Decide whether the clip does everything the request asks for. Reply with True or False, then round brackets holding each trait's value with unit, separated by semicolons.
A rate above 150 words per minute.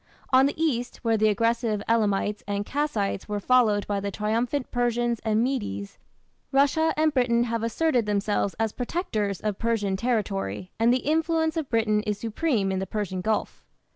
True (170 wpm)